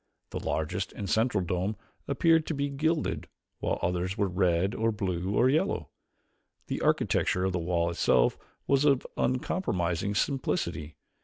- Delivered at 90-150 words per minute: Yes, average, 145 wpm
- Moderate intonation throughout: No, wide, 6.9 semitones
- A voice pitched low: Yes, low, 100 Hz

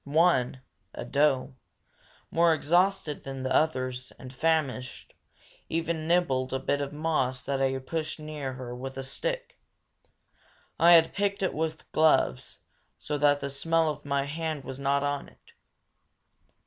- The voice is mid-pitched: Yes, medium, 145 Hz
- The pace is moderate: Yes, average, 150 wpm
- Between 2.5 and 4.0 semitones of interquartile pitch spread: Yes, average, 3.5 semitones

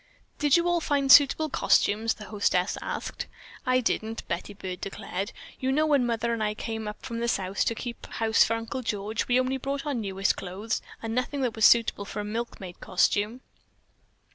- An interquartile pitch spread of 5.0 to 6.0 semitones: No, average, 3.7 semitones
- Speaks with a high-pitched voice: Yes, high, 225 Hz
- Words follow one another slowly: No, average, 190 wpm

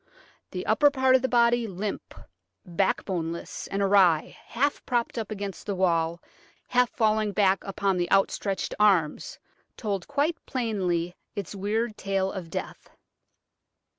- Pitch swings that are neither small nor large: Yes, average, 4.0 semitones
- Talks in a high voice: Yes, high, 200 Hz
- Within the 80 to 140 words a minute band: Yes, slow, 135 wpm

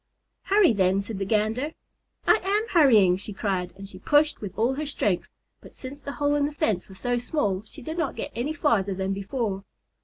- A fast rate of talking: Yes, fast, 210 wpm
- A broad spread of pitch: Yes, wide, 7.0 semitones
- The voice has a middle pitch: No, high, 225 Hz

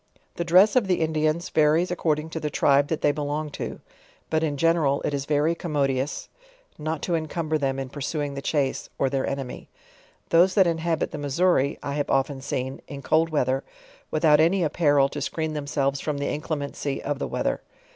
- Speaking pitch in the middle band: Yes, medium, 150 Hz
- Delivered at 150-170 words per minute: No, average, 195 wpm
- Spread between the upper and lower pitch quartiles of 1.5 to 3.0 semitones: Yes, narrow, 2.5 semitones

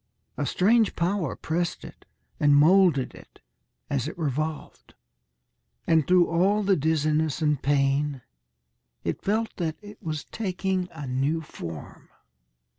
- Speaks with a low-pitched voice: No, medium, 160 Hz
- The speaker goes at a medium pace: No, slow, 125 wpm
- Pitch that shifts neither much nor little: Yes, average, 4.1 semitones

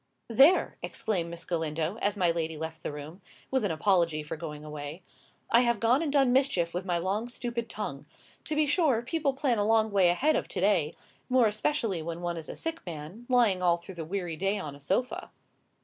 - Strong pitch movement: Yes, wide, 6.5 semitones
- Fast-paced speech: Yes, fast, 210 wpm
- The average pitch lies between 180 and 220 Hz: Yes, high, 190 Hz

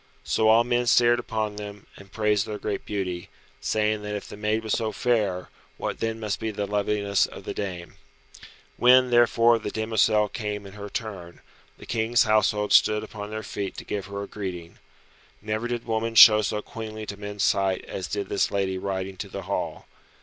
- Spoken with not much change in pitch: Yes, narrow, 1.8 semitones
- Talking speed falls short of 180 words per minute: No, average, 190 wpm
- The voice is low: Yes, low, 105 Hz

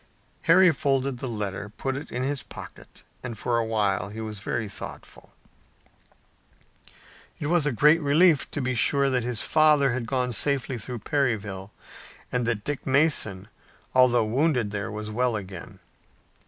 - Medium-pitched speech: No, low, 125 Hz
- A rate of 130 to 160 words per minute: Yes, average, 155 wpm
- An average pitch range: Yes, average, 4.6 semitones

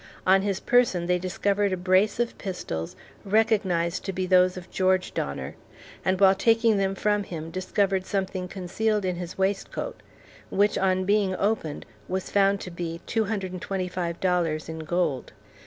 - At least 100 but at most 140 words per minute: No, average, 150 wpm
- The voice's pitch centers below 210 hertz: Yes, medium, 185 Hz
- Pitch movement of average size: No, narrow, 2.0 semitones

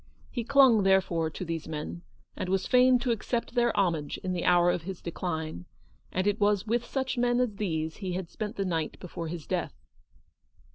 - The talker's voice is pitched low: No, high, 190 Hz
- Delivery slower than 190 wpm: No, average, 200 wpm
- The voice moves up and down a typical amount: No, wide, 5.7 semitones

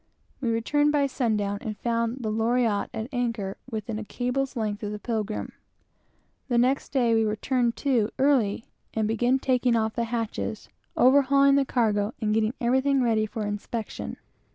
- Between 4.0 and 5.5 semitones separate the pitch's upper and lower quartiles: No, average, 2.9 semitones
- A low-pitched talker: No, high, 230 Hz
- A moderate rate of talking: Yes, average, 170 wpm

